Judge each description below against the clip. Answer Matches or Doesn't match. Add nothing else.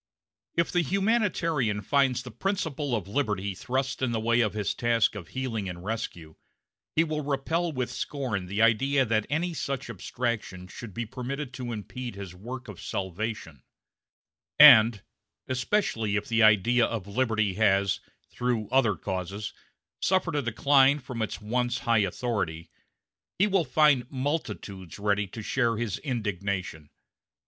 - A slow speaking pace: Doesn't match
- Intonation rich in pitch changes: Doesn't match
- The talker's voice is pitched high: Doesn't match